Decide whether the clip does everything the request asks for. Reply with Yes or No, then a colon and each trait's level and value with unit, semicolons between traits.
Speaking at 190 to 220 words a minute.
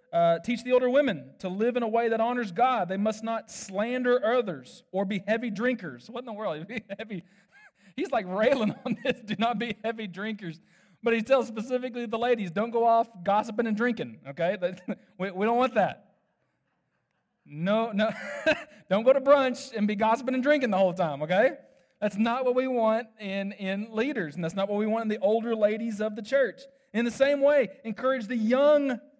Yes: fast, 205 wpm